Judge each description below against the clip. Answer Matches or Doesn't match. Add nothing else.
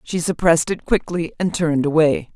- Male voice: Doesn't match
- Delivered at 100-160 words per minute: Doesn't match